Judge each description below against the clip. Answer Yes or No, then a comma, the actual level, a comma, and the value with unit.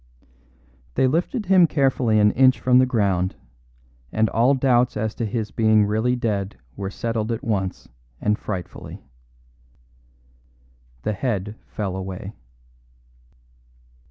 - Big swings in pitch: No, average, 3.6 semitones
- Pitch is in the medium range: No, low, 110 Hz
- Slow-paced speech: Yes, slow, 120 wpm